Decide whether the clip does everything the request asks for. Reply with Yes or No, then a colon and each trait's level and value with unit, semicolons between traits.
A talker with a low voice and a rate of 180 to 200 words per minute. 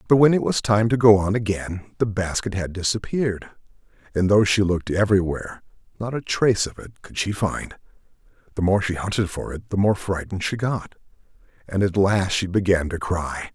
Yes: low, 100 Hz; average, 195 wpm